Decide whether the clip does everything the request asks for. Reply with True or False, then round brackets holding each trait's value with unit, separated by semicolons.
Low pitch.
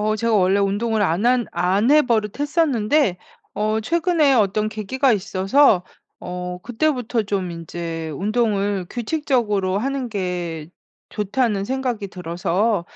False (210 Hz)